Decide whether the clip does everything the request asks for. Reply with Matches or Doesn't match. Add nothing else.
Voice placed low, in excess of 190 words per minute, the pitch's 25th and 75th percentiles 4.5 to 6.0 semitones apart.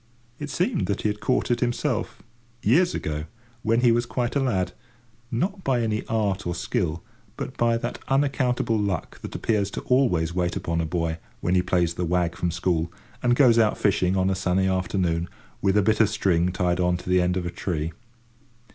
Matches